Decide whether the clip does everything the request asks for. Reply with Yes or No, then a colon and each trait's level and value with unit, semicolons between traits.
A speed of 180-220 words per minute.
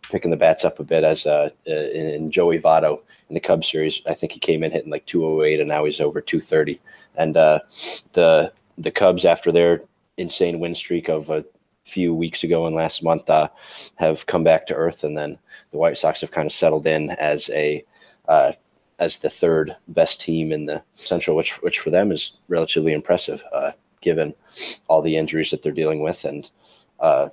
Yes: average, 200 wpm